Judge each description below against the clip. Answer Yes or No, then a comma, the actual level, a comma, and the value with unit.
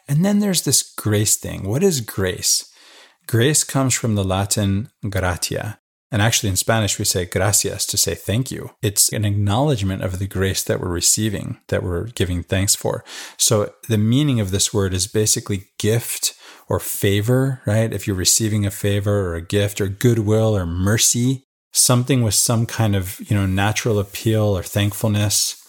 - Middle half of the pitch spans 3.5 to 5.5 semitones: No, average, 2.8 semitones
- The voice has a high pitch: No, low, 105 Hz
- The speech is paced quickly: No, average, 175 wpm